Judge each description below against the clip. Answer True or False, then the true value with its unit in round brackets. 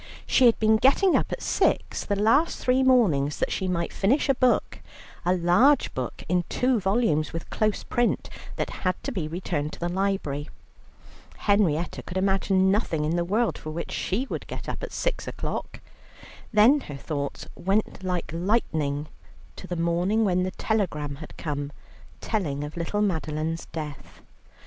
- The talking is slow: False (170 wpm)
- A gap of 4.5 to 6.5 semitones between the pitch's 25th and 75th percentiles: True (5.6 semitones)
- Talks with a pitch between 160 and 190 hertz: True (185 Hz)